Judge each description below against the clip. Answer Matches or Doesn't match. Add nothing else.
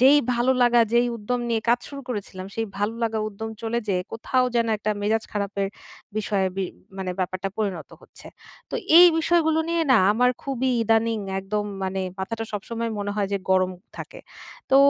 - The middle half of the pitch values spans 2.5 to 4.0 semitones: Matches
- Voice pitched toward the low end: Doesn't match